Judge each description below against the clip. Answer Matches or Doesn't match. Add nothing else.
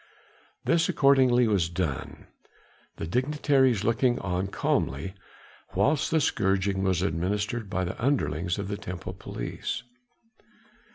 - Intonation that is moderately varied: Doesn't match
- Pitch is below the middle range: Matches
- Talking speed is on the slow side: Matches